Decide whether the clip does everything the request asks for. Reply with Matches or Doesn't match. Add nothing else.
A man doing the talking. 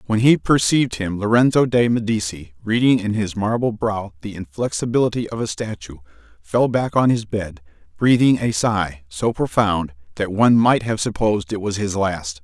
Matches